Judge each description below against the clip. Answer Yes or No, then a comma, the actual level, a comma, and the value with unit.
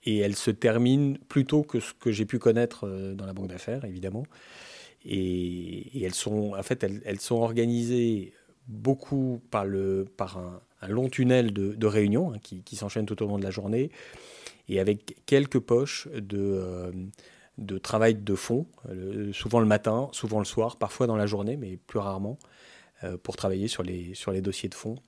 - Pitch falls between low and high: No, low, 105 Hz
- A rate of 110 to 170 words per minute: No, average, 185 wpm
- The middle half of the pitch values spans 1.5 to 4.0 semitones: Yes, average, 3.6 semitones